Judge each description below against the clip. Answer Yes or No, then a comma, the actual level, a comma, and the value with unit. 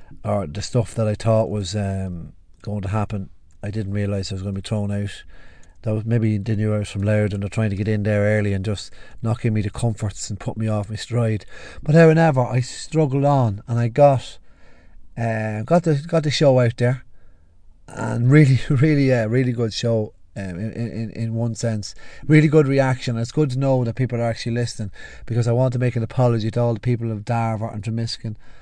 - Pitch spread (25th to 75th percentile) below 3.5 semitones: Yes, average, 3.0 semitones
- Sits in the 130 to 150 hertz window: No, low, 115 Hz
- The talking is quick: Yes, fast, 225 wpm